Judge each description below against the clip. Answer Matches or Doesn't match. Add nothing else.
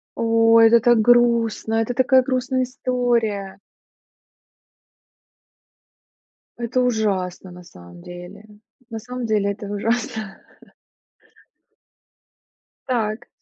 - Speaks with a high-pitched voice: Matches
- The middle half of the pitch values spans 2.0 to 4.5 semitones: Matches